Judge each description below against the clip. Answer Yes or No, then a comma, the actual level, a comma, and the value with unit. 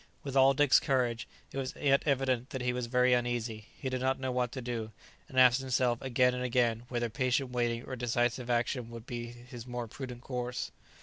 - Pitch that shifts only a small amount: Yes, narrow, 1.5 semitones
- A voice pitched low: Yes, low, 125 Hz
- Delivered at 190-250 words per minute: Yes, fast, 205 wpm